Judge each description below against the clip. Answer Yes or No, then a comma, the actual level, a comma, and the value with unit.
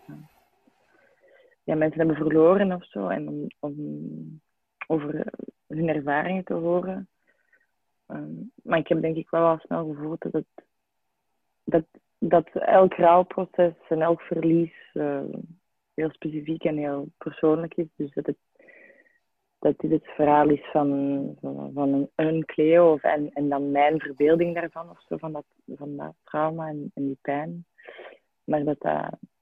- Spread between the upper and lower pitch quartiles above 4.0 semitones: No, narrow, 2.4 semitones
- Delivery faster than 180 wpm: No, average, 150 wpm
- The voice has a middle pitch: Yes, medium, 160 Hz